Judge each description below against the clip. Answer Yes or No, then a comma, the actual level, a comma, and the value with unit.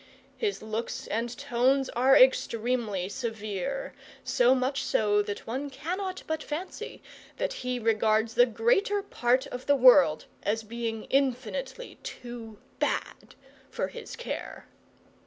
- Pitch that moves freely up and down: No, average, 3.7 semitones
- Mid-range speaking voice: No, high, 245 Hz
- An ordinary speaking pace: No, slow, 125 wpm